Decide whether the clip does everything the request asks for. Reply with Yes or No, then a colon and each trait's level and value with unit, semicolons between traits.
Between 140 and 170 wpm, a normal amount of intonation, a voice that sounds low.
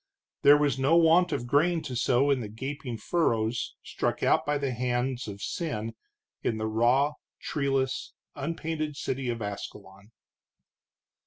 Yes: average, 145 wpm; average, 4.3 semitones; low, 130 Hz